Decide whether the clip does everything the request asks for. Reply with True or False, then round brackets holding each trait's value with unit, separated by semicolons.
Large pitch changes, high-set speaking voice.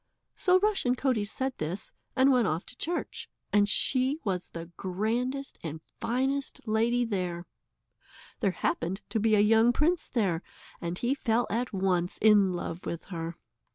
True (5.8 semitones; 220 Hz)